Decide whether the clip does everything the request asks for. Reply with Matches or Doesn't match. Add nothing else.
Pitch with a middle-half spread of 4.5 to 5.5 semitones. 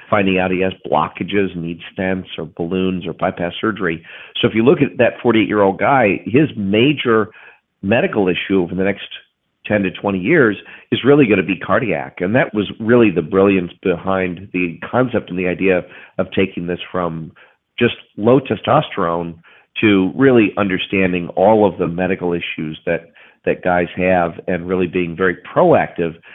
Doesn't match